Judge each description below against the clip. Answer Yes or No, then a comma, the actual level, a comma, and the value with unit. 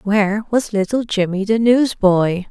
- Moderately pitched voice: No, high, 210 Hz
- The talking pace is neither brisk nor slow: Yes, average, 145 wpm